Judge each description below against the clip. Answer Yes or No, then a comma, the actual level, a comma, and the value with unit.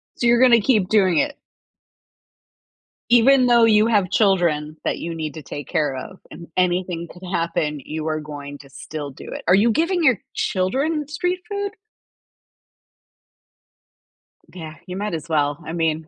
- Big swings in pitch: Yes, wide, 7.1 semitones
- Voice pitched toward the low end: No, medium, 180 Hz